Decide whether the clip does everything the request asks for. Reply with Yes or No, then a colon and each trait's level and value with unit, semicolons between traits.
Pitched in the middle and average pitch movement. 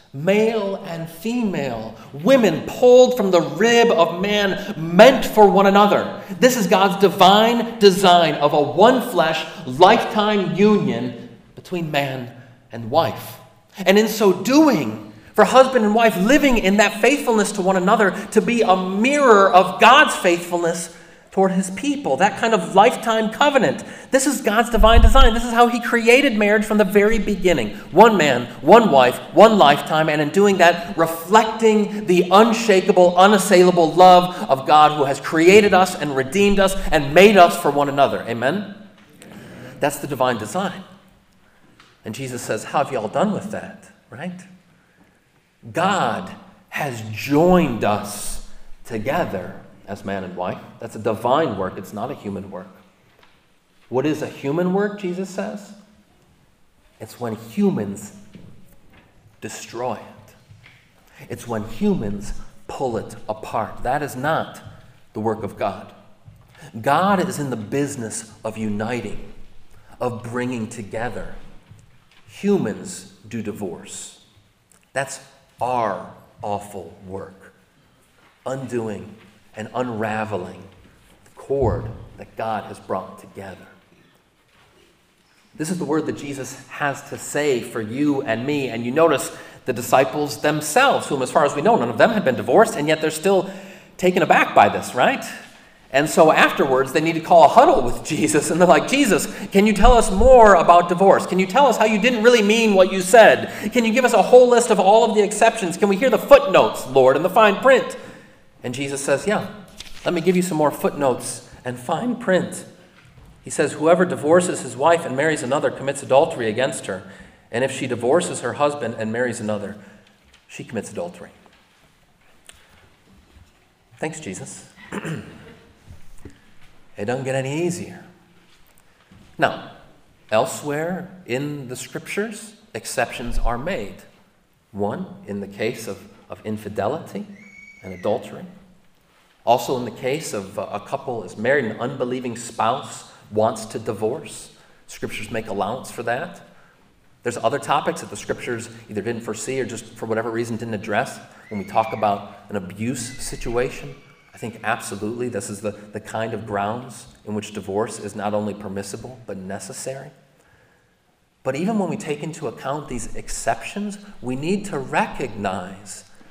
No: medium, 165 Hz; wide, 9.0 semitones